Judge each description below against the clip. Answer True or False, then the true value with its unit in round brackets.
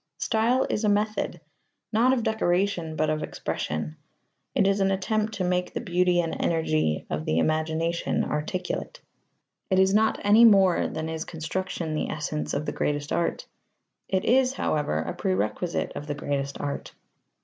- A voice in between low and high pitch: True (175 Hz)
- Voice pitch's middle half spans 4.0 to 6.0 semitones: True (4.9 semitones)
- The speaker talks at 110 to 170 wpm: True (160 wpm)